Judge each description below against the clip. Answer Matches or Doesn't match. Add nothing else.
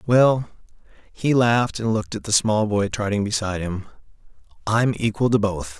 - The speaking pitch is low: Matches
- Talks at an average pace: Matches